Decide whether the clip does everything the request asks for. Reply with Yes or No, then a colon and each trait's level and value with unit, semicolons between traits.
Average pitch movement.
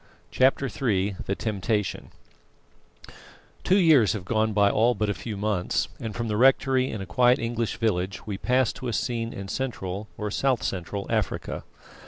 Yes: average, 3.6 semitones